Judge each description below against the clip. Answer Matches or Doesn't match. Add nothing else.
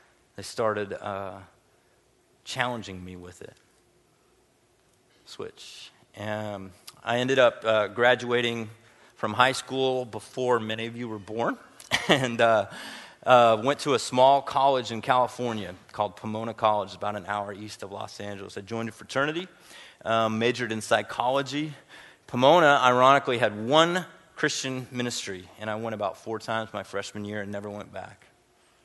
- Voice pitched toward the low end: Matches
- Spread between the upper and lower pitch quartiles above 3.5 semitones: Doesn't match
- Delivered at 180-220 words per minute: Doesn't match